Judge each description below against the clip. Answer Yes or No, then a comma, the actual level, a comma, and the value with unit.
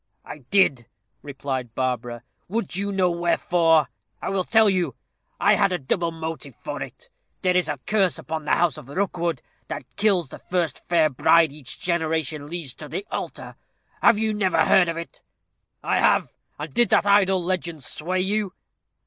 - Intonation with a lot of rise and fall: No, average, 4.0 semitones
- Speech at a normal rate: Yes, average, 175 wpm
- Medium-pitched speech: Yes, medium, 170 Hz